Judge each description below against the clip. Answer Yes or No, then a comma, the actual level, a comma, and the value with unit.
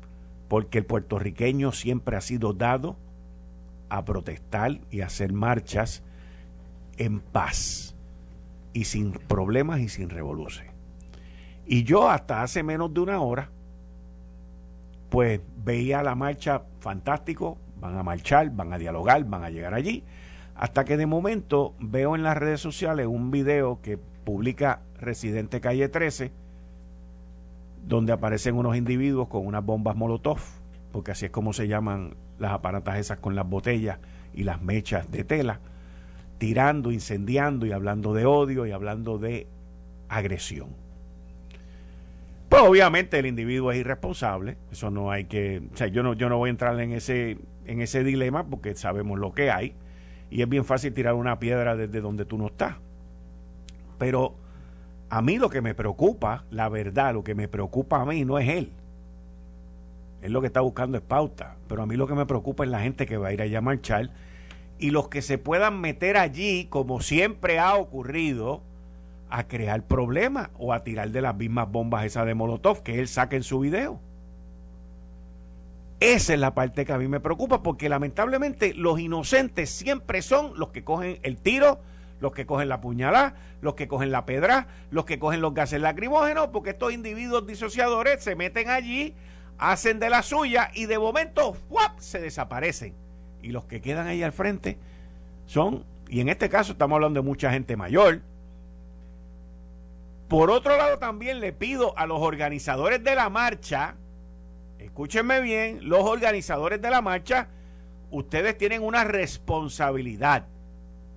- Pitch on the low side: Yes, low, 115 Hz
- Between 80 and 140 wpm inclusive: No, average, 165 wpm